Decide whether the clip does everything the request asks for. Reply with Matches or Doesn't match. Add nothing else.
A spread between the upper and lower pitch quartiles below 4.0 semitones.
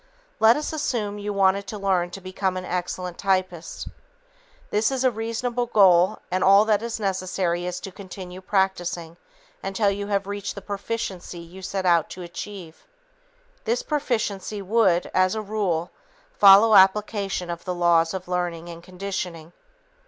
Matches